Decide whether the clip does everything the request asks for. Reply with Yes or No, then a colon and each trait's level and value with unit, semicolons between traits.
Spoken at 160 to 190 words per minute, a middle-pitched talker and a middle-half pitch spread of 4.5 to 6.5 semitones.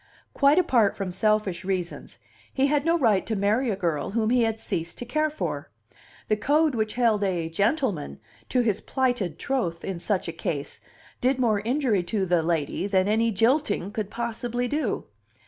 No: average, 180 wpm; high, 215 Hz; average, 5.1 semitones